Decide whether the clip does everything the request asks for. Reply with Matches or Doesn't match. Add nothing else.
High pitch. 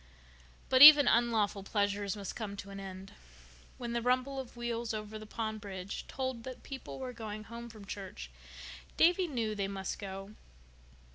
Matches